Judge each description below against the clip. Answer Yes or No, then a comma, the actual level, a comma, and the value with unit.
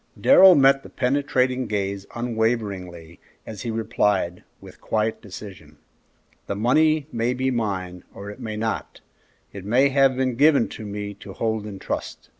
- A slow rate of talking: No, average, 150 wpm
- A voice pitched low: Yes, low, 110 Hz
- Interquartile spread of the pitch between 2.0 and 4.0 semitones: No, average, 4.5 semitones